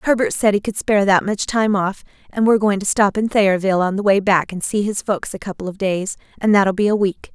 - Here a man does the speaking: No, female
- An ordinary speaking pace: No, fast, 270 wpm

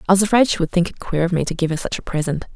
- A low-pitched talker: No, medium, 175 Hz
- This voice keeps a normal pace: No, fast, 375 wpm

